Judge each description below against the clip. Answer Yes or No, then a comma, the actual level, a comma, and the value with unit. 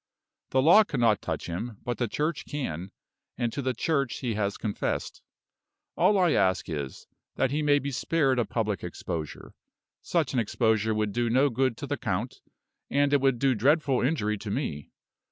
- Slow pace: No, average, 180 wpm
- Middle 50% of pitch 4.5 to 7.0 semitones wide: Yes, average, 4.9 semitones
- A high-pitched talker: No, low, 125 Hz